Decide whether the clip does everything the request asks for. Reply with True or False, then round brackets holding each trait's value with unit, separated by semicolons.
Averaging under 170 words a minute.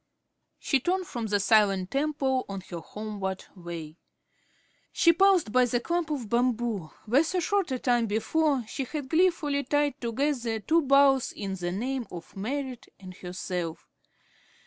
True (150 wpm)